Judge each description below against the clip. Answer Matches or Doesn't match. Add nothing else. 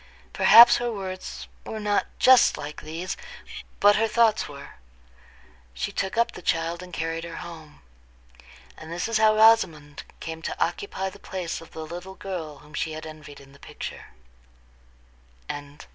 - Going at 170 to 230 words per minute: Doesn't match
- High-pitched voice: Doesn't match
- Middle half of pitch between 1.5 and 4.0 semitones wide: Doesn't match